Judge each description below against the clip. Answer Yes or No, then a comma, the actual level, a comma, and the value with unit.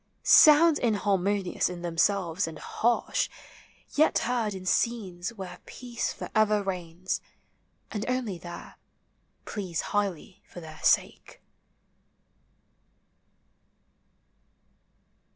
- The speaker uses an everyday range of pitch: Yes, average, 4.4 semitones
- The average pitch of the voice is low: No, high, 200 Hz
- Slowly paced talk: Yes, slow, 90 wpm